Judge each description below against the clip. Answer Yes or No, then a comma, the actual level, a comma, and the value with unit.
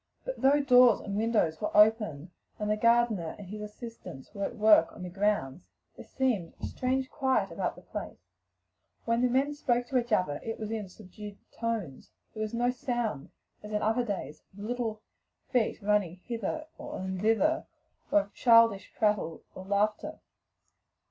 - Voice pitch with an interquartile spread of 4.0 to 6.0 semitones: No, average, 3.3 semitones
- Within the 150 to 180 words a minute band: Yes, average, 165 wpm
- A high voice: Yes, high, 215 Hz